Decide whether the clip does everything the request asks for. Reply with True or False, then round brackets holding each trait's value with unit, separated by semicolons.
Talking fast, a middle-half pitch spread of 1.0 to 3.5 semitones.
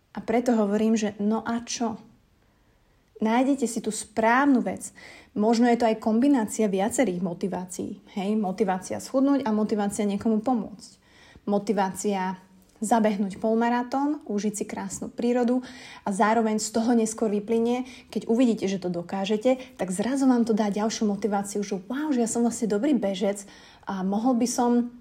False (150 wpm; 2.8 semitones)